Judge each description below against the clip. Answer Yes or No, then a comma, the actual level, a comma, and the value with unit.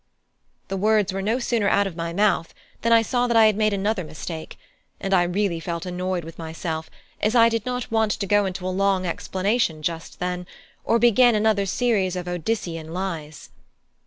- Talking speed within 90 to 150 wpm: No, average, 190 wpm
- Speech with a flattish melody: No, average, 3.9 semitones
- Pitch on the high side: Yes, high, 195 Hz